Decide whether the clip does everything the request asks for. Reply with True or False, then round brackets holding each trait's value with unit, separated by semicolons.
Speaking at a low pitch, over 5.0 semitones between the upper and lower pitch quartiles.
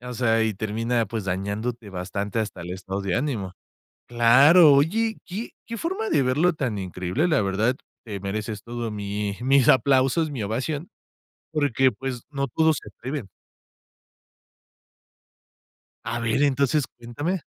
True (120 Hz; 5.5 semitones)